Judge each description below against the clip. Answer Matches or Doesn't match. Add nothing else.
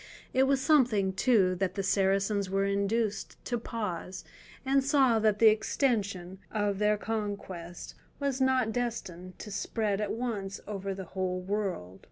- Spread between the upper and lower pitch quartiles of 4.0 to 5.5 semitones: Doesn't match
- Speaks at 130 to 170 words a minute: Matches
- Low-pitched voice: Doesn't match